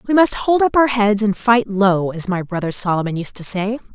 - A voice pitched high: Yes, high, 210 Hz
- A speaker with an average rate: No, fast, 245 wpm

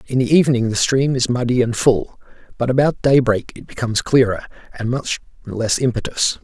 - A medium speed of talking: Yes, average, 175 wpm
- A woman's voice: No, male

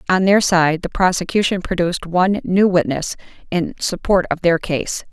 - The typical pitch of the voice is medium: Yes, medium, 180 Hz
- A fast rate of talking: No, average, 165 wpm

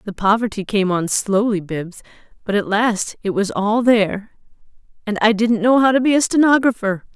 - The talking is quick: No, average, 175 wpm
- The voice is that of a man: No, female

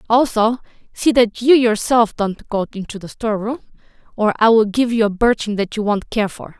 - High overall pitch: Yes, high, 220 Hz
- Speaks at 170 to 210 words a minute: Yes, average, 200 wpm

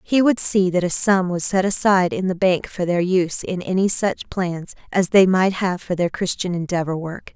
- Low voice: No, medium, 185 Hz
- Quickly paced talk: Yes, fast, 230 wpm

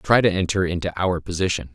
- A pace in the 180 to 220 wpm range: Yes, fast, 205 wpm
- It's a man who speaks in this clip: Yes, male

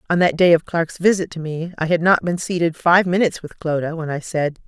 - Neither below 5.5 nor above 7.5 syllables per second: Yes, 5.8 syllables/s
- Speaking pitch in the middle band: Yes, medium, 170 Hz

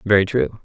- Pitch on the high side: No, low, 100 Hz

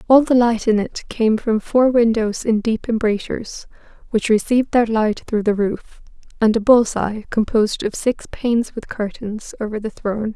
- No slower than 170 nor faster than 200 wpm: Yes, average, 185 wpm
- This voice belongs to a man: No, female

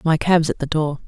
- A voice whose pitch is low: No, medium, 155 Hz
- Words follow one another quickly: Yes, fast, 280 wpm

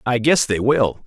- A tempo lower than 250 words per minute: Yes, fast, 225 wpm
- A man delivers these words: Yes, male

